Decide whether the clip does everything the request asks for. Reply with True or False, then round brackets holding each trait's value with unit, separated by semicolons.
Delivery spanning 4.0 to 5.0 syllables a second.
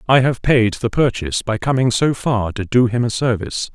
False (5.3 syllables/s)